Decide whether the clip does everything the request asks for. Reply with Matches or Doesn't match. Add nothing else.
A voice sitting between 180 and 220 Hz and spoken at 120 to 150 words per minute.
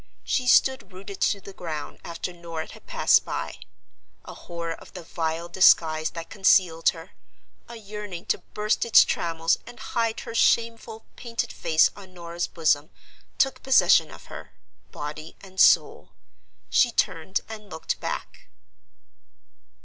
Matches